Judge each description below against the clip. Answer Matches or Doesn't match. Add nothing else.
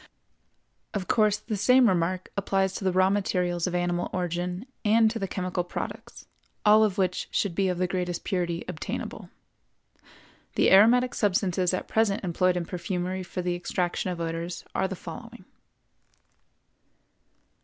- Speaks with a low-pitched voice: Doesn't match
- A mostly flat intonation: Matches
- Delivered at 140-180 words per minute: Matches